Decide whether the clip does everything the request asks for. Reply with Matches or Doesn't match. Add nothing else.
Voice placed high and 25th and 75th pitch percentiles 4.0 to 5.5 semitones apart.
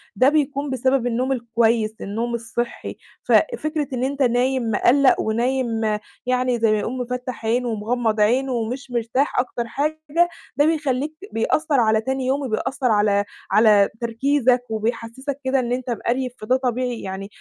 Doesn't match